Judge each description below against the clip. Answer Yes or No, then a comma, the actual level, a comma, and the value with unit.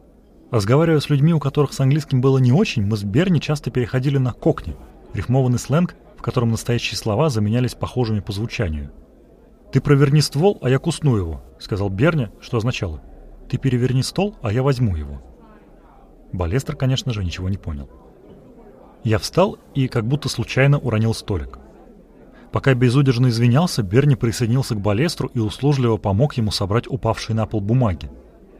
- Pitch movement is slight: No, average, 4.2 semitones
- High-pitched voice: No, low, 125 Hz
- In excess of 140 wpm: Yes, fast, 160 wpm